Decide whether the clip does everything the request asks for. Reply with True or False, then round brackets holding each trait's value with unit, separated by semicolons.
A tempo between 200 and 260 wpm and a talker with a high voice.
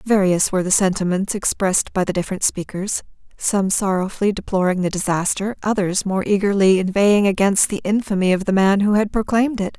False (165 wpm; 195 Hz)